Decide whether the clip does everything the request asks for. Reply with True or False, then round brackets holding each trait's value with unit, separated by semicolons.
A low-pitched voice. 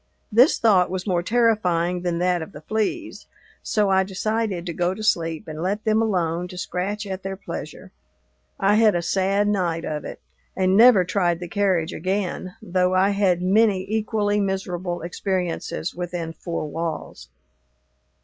False (185 Hz)